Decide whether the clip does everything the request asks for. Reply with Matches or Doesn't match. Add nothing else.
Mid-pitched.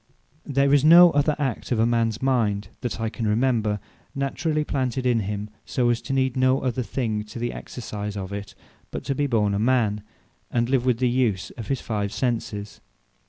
Doesn't match